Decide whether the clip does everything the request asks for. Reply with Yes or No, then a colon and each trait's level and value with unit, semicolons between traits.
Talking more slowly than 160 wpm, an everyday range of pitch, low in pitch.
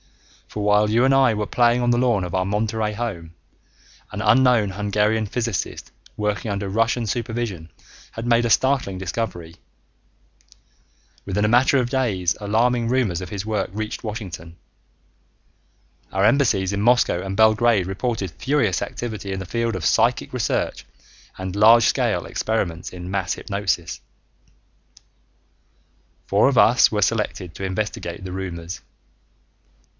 Yes: average, 140 wpm; average, 3.7 semitones; low, 105 Hz